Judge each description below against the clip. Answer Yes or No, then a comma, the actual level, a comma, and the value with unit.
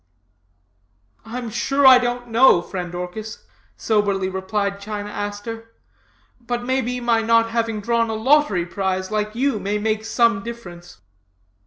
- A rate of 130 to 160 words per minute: Yes, average, 140 wpm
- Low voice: No, high, 220 Hz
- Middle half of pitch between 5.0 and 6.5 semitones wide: No, average, 2.8 semitones